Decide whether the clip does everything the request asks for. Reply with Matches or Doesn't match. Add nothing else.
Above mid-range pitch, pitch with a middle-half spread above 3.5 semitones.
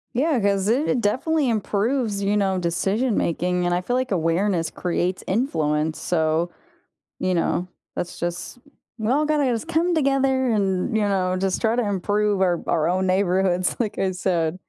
Matches